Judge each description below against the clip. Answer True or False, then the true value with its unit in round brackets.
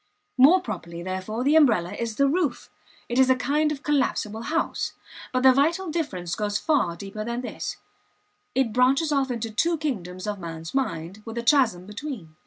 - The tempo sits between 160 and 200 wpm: True (180 wpm)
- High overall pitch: True (240 Hz)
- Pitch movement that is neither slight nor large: False (6.1 semitones)